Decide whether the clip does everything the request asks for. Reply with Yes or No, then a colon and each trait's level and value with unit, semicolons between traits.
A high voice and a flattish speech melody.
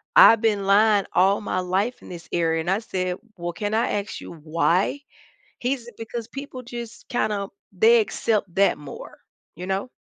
No: high, 200 Hz; average, 3.9 semitones